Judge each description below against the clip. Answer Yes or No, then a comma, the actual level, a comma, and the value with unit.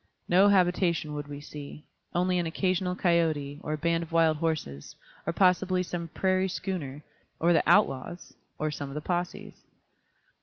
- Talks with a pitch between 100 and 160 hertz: No, medium, 170 Hz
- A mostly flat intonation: No, average, 3.3 semitones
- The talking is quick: No, average, 160 wpm